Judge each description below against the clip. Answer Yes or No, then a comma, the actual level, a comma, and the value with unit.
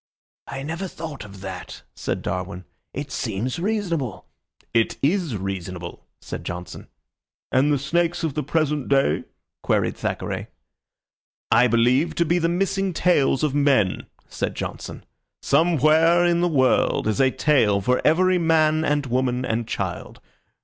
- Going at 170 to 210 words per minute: No, average, 140 wpm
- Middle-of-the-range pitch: Yes, medium, 145 Hz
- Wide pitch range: Yes, wide, 6.0 semitones